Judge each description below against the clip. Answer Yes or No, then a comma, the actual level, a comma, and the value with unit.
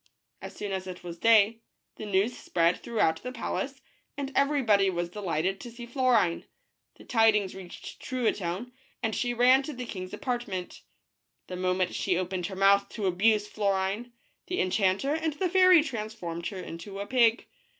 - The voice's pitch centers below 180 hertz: No, high, 210 Hz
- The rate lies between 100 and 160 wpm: No, average, 170 wpm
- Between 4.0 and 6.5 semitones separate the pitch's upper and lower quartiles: Yes, average, 4.8 semitones